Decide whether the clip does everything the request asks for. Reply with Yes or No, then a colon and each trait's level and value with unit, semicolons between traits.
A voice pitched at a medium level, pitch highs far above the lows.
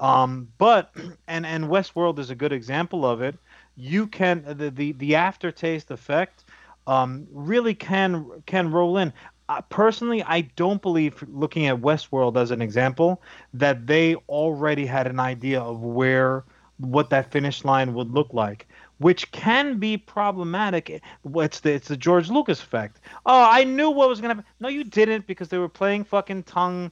Yes: medium, 160 Hz; wide, 5.8 semitones